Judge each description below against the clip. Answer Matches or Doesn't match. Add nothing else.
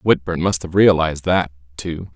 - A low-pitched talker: Matches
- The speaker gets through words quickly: Doesn't match